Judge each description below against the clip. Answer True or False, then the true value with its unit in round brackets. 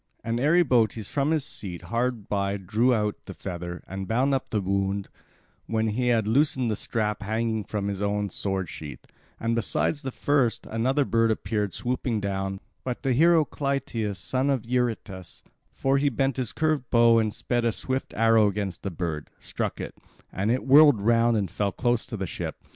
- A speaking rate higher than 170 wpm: True (180 wpm)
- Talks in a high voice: False (115 Hz)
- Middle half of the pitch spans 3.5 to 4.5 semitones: True (4.1 semitones)